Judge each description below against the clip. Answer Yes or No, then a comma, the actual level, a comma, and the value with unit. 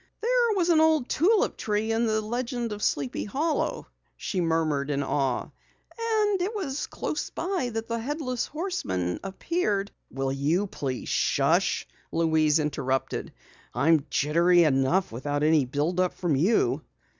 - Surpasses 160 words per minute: No, average, 145 wpm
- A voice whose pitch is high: Yes, high, 195 Hz